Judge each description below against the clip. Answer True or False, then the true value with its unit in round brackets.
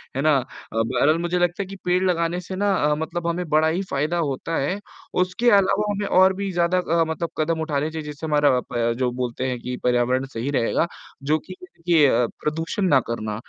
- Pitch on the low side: False (160 Hz)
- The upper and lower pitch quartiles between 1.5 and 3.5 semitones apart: False (4.8 semitones)